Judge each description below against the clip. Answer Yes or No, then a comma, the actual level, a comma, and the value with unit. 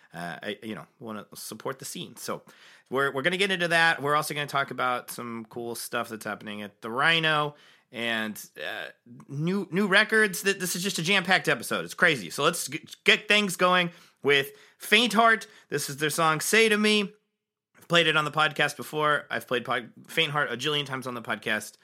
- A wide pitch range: Yes, wide, 6.7 semitones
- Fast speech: Yes, fast, 210 wpm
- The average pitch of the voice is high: No, medium, 155 Hz